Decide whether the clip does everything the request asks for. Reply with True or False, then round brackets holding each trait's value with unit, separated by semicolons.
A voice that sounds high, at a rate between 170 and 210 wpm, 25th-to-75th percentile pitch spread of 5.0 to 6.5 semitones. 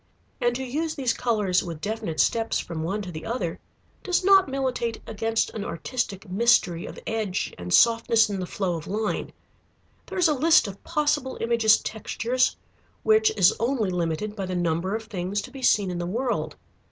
True (220 Hz; 185 wpm; 5.5 semitones)